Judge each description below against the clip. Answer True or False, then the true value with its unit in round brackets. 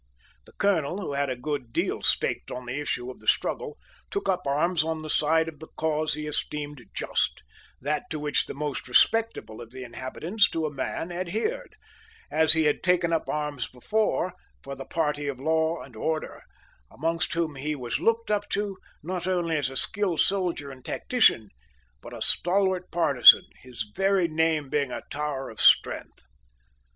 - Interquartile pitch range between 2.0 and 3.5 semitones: False (4.3 semitones)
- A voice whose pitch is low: False (155 Hz)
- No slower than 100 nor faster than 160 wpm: False (180 wpm)